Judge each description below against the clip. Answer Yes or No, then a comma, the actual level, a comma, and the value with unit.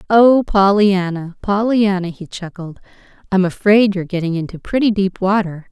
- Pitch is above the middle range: Yes, high, 195 Hz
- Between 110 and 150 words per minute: Yes, slow, 135 wpm